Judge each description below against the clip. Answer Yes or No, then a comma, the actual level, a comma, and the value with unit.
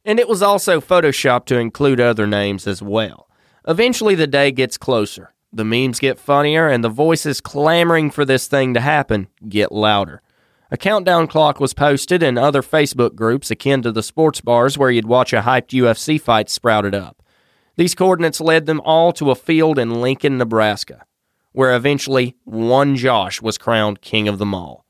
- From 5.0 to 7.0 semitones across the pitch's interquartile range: Yes, wide, 5.5 semitones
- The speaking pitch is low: Yes, low, 130 Hz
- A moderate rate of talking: Yes, average, 180 wpm